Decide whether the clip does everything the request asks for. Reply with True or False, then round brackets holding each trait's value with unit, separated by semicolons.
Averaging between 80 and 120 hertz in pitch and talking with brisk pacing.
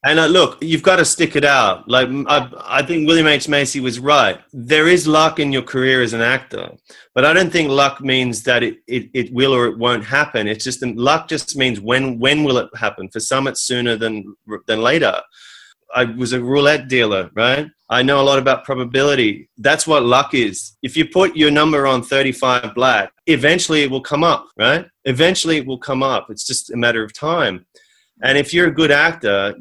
False (135 Hz; 230 wpm)